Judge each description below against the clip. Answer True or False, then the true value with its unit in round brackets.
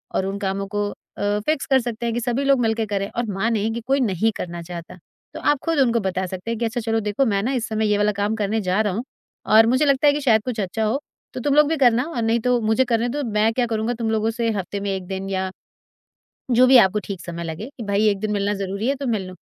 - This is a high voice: True (220 Hz)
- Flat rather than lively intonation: False (3.3 semitones)